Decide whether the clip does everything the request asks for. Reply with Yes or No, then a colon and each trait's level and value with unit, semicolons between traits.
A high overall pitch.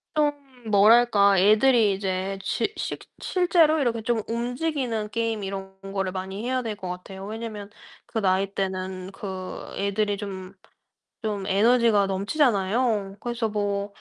Yes: high, 205 Hz